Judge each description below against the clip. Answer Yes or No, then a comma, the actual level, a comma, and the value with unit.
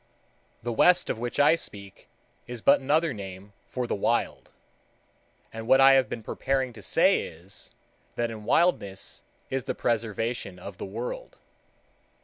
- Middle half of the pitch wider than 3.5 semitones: Yes, average, 4.6 semitones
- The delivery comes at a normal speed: Yes, average, 150 wpm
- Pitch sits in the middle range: No, low, 115 Hz